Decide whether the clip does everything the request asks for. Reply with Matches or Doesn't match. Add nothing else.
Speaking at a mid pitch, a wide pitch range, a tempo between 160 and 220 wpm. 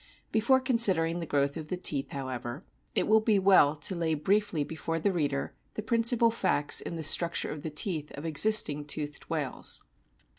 Matches